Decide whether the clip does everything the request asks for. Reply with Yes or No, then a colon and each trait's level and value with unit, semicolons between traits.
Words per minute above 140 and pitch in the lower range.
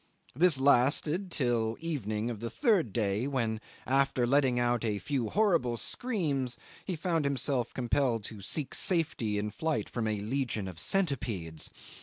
Yes: average, 155 wpm; low, 125 Hz